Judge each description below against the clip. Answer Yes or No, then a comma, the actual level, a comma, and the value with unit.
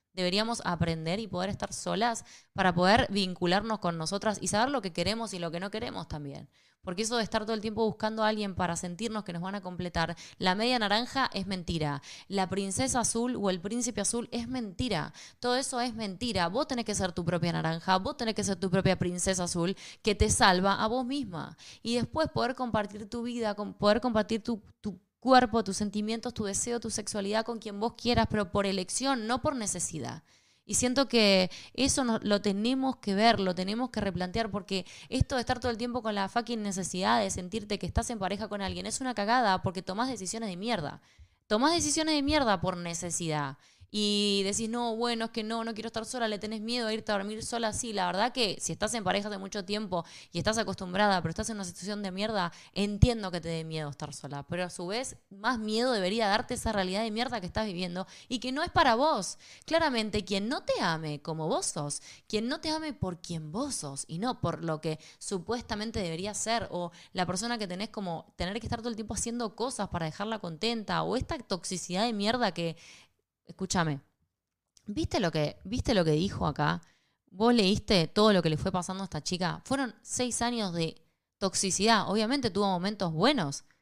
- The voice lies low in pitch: No, high, 205 Hz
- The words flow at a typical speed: No, fast, 210 wpm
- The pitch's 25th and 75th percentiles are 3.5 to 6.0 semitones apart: Yes, average, 4.2 semitones